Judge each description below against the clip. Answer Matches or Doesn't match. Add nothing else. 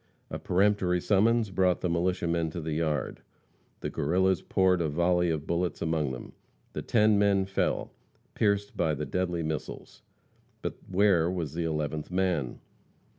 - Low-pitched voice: Matches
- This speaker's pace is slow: Doesn't match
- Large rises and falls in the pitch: Doesn't match